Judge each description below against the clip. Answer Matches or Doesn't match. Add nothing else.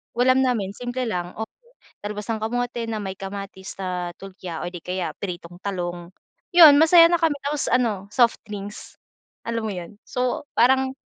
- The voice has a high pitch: Matches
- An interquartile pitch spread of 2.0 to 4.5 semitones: Doesn't match